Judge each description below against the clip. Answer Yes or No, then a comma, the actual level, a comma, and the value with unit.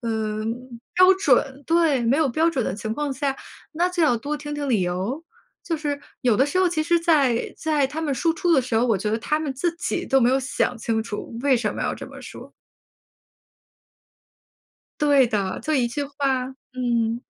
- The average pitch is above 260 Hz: Yes, very high, 270 Hz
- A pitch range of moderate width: Yes, average, 4.9 semitones